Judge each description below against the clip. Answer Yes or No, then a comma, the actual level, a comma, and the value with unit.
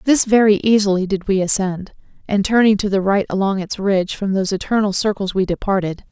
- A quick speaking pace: No, average, 195 wpm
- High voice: Yes, high, 200 Hz